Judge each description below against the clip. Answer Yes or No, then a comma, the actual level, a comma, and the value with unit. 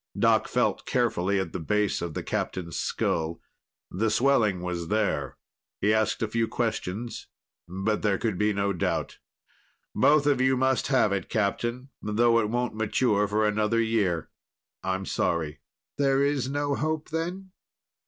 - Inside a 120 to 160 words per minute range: Yes, average, 150 wpm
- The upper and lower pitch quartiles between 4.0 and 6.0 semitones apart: Yes, average, 4.5 semitones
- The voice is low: Yes, low, 110 Hz